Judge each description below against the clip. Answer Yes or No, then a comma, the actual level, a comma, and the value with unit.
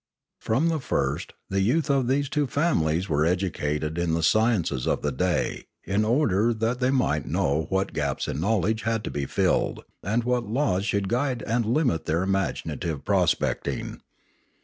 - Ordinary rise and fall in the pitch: No, wide, 6.9 semitones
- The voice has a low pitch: Yes, low, 100 Hz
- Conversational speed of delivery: Yes, average, 170 wpm